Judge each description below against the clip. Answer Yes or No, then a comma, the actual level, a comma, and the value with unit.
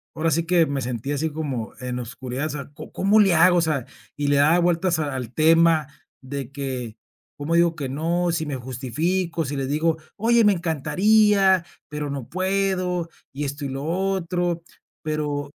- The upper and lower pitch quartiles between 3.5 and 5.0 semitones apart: Yes, average, 4.0 semitones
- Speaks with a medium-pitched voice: Yes, medium, 155 Hz